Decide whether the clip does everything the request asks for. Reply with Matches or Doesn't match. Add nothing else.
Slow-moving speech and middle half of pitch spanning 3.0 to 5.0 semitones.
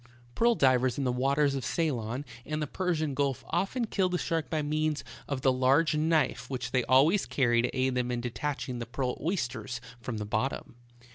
Doesn't match